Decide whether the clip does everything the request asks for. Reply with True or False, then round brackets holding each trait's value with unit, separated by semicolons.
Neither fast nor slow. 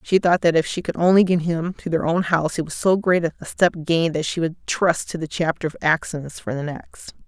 False (265 wpm)